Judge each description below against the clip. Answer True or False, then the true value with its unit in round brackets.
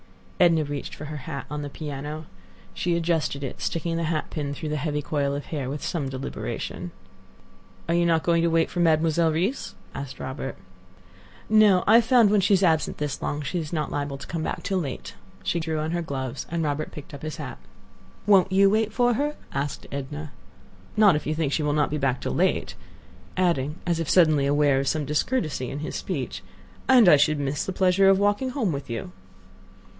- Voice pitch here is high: False (155 Hz)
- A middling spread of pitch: True (3.7 semitones)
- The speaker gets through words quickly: True (210 wpm)